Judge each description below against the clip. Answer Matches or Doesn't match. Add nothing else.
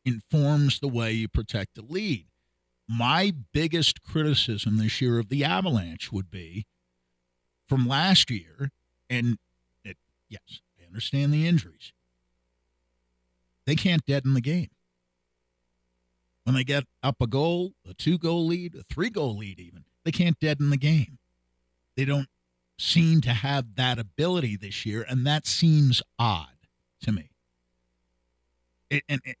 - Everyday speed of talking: Matches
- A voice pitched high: Doesn't match